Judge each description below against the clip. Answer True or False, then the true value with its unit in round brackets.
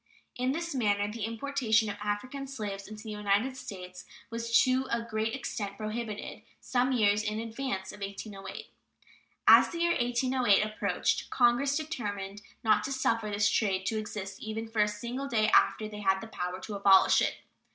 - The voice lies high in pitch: True (220 Hz)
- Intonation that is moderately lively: True (3.2 semitones)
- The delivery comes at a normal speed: True (170 wpm)